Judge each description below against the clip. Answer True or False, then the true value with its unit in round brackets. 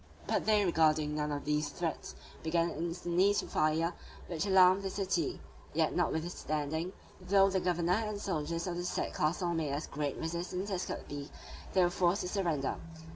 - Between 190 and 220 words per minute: False (165 wpm)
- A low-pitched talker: False (170 Hz)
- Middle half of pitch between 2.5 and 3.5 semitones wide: True (3.2 semitones)